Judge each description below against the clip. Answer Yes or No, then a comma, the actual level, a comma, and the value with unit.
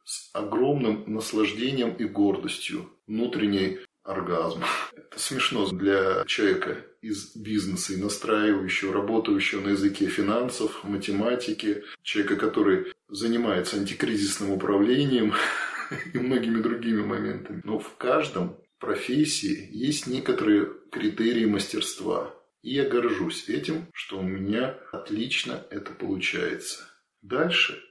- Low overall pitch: Yes, low, 110 Hz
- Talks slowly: Yes, slow, 105 wpm